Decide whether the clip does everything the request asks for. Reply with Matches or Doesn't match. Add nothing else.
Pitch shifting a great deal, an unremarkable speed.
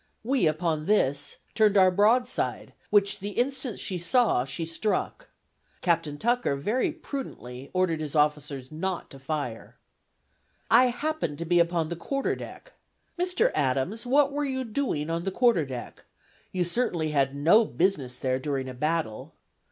Matches